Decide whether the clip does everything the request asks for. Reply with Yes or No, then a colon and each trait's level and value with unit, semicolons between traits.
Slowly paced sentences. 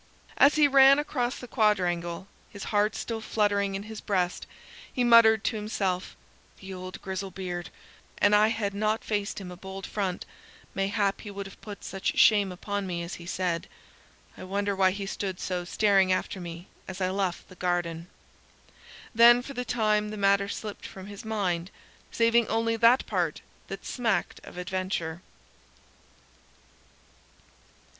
No: average, 160 wpm